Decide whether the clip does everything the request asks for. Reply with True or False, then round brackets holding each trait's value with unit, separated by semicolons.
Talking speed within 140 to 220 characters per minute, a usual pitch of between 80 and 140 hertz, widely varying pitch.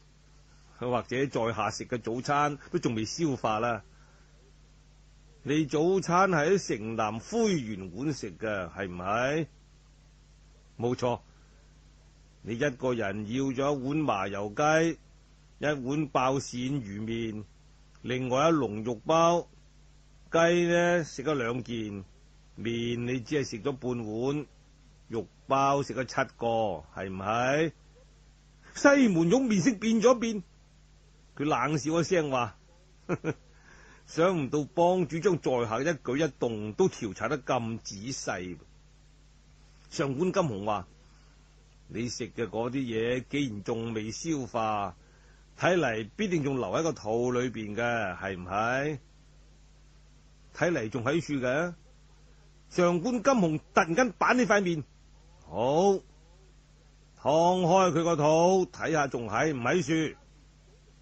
True (170 characters per minute; 135 Hz; 6.4 semitones)